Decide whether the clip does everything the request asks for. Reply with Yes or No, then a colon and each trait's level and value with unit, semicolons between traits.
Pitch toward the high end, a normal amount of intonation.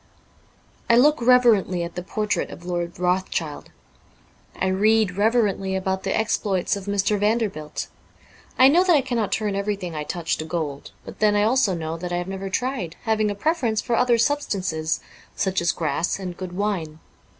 Yes: high, 195 Hz; average, 4.0 semitones